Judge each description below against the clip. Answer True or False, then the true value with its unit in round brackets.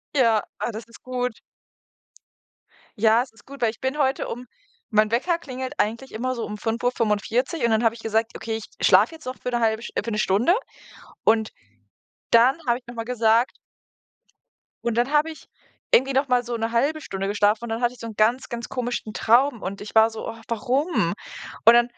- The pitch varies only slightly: True (2.3 semitones)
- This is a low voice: False (235 Hz)